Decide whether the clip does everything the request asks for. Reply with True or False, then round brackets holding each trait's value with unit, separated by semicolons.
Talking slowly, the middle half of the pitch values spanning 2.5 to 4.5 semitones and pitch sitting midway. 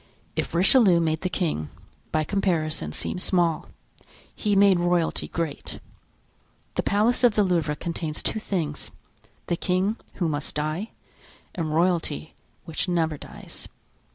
True (125 wpm; 3.5 semitones; 175 Hz)